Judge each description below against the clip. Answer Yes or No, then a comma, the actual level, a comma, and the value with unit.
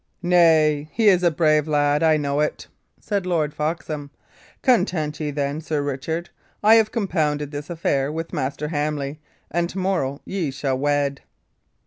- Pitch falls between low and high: Yes, medium, 150 Hz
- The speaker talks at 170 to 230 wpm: No, average, 155 wpm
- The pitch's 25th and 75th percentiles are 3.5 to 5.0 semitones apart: No, average, 2.9 semitones